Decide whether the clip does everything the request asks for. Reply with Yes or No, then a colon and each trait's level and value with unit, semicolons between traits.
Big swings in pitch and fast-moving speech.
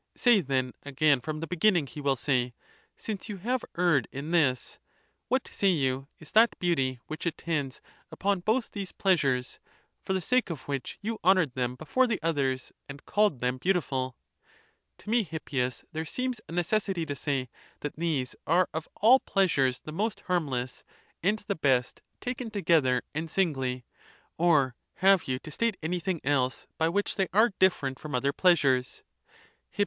No: wide, 6.4 semitones; average, 170 wpm